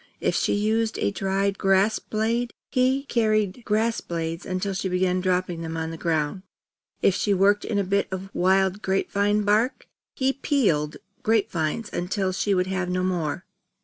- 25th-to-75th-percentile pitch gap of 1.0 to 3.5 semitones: Yes, average, 2.8 semitones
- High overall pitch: Yes, high, 195 Hz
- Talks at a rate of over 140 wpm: Yes, average, 175 wpm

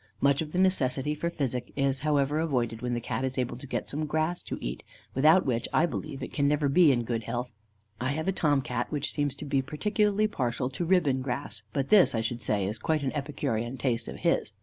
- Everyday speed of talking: No, fast, 235 wpm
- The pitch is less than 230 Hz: Yes, medium, 140 Hz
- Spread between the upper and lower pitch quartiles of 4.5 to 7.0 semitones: No, average, 3.9 semitones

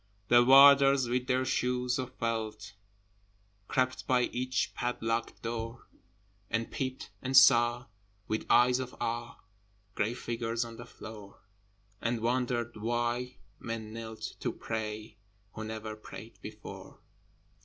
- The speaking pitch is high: No, low, 120 Hz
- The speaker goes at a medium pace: No, slow, 120 wpm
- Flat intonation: Yes, narrow, 1.9 semitones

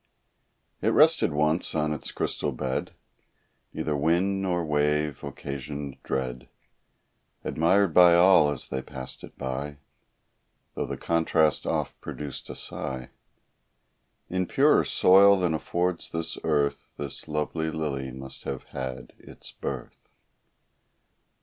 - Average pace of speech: No, slow, 120 wpm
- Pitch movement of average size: Yes, average, 3.8 semitones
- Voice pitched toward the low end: Yes, very low, 75 Hz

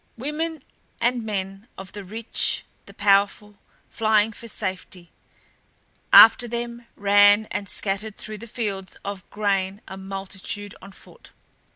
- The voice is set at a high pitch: Yes, high, 205 Hz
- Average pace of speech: No, slow, 130 wpm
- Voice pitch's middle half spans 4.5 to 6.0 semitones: No, narrow, 2.5 semitones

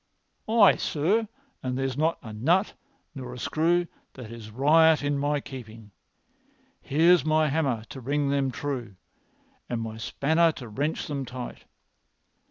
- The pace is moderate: Yes, average, 150 wpm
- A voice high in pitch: No, medium, 140 Hz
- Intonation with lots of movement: No, average, 4.2 semitones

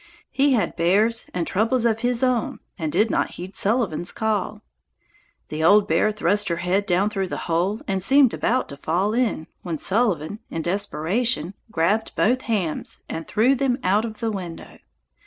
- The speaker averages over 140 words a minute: Yes, average, 175 wpm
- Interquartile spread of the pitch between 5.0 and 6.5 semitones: No, average, 4.5 semitones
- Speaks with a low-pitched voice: No, high, 205 Hz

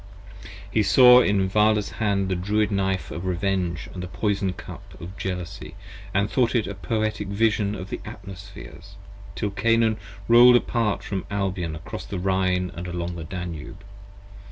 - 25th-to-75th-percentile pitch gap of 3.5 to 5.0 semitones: No, average, 2.7 semitones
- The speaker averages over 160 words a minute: No, average, 155 wpm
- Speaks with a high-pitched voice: No, low, 100 Hz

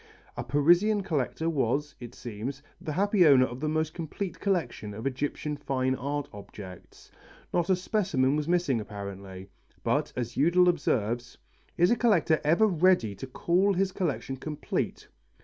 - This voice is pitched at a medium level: Yes, medium, 150 Hz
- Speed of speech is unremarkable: Yes, average, 150 wpm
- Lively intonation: Yes, wide, 5.9 semitones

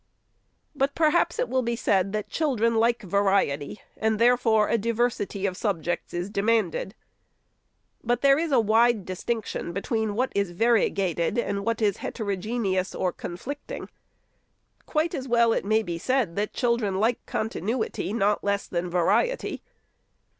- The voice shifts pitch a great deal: No, average, 3.5 semitones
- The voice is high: Yes, high, 220 Hz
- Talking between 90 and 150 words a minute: Yes, average, 145 wpm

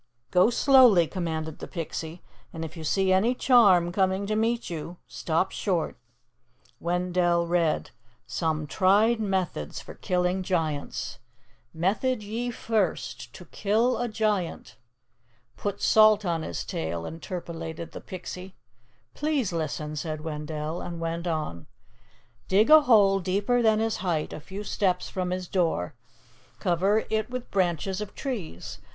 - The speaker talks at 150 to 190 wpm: No, average, 140 wpm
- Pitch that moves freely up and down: No, average, 4.4 semitones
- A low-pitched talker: No, medium, 180 Hz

